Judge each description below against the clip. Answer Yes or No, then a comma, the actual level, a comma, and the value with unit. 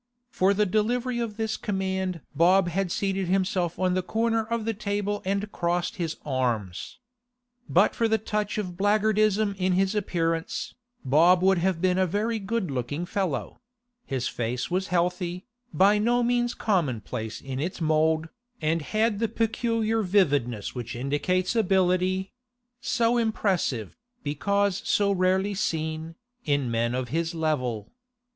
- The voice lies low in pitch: No, medium, 185 Hz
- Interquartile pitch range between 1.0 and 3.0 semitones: No, average, 4.8 semitones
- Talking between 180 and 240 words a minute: No, average, 145 wpm